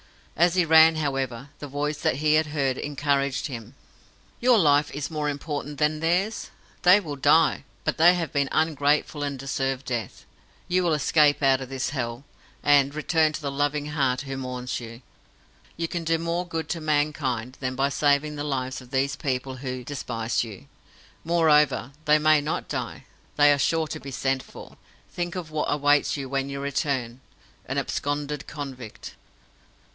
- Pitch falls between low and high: Yes, medium, 145 Hz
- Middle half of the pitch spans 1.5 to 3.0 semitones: Yes, narrow, 2.5 semitones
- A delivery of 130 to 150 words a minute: No, average, 175 wpm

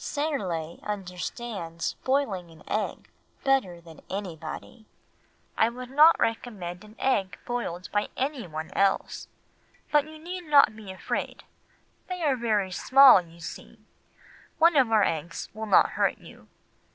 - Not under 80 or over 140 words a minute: Yes, slow, 135 wpm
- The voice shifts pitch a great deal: Yes, wide, 7.1 semitones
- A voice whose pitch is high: Yes, high, 215 Hz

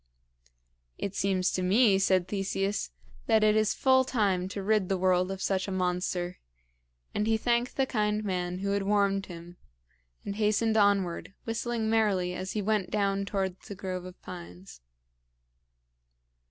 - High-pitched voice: Yes, high, 195 Hz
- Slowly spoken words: No, average, 155 wpm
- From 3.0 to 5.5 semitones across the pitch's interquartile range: No, narrow, 2.6 semitones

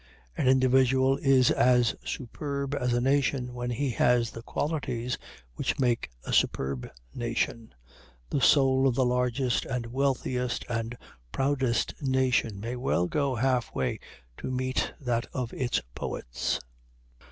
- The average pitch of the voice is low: Yes, low, 125 Hz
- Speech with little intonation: Yes, narrow, 1.9 semitones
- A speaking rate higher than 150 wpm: No, slow, 135 wpm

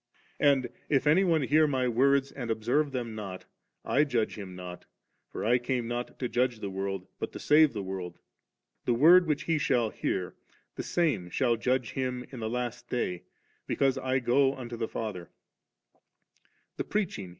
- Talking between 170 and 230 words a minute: Yes, average, 180 wpm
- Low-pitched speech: Yes, low, 125 Hz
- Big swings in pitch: No, average, 4.0 semitones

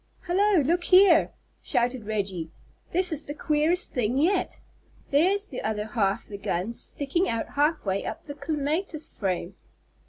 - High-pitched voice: Yes, very high, 290 Hz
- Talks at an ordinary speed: Yes, average, 150 wpm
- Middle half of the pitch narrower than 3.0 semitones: No, wide, 8.1 semitones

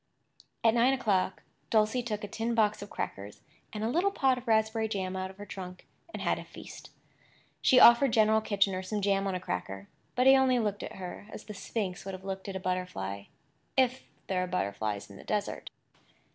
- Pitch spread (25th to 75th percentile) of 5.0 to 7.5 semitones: No, average, 3.6 semitones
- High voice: Yes, high, 205 Hz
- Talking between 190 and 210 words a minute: Yes, average, 200 wpm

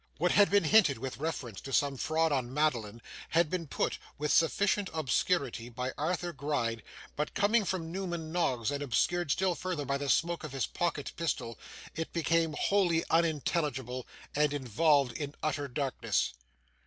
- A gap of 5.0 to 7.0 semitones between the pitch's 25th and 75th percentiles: No, average, 4.1 semitones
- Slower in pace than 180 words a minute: Yes, average, 160 wpm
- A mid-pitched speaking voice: Yes, medium, 150 Hz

